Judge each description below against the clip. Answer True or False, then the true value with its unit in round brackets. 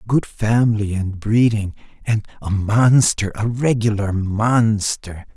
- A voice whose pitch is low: True (110 Hz)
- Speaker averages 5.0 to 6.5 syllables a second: False (3.8 syllables/s)